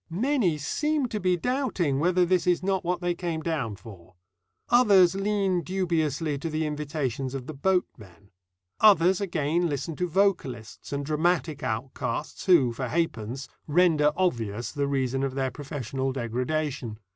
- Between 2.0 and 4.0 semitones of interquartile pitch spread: No, average, 5.3 semitones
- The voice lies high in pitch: No, medium, 155 Hz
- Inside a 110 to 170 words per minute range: Yes, average, 145 wpm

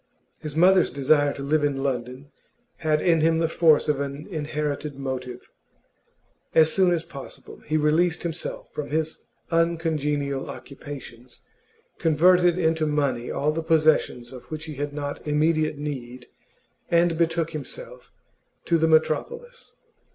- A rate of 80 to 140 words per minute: Yes, slow, 135 wpm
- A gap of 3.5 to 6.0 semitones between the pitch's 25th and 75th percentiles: No, narrow, 2.5 semitones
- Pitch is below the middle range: No, medium, 155 Hz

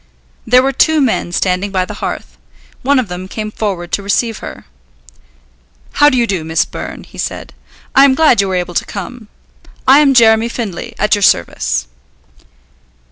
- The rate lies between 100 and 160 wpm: No, average, 180 wpm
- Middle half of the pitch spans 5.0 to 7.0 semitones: Yes, wide, 5.6 semitones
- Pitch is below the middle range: No, high, 215 Hz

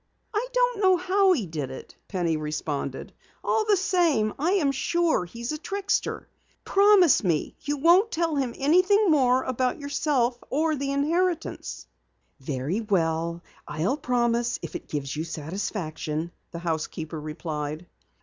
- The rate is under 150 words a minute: Yes, average, 140 wpm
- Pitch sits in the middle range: No, very high, 250 Hz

